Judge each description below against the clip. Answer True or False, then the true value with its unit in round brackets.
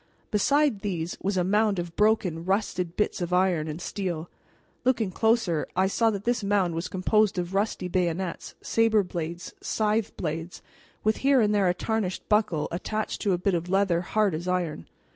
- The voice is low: False (190 Hz)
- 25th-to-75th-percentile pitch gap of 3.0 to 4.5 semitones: True (3.5 semitones)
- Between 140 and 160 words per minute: False (180 wpm)